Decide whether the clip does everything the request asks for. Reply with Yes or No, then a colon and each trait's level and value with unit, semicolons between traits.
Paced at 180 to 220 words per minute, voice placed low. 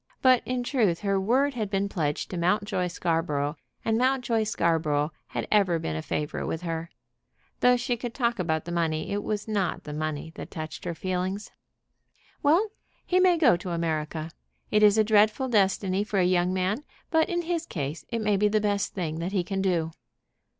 No: average, 190 wpm; high, 195 Hz